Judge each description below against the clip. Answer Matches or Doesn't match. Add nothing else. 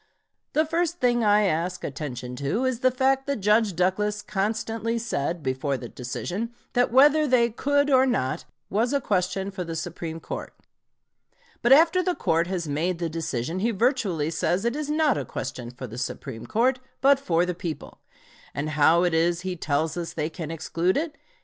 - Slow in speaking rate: Doesn't match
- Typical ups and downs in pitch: Doesn't match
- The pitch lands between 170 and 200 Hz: Matches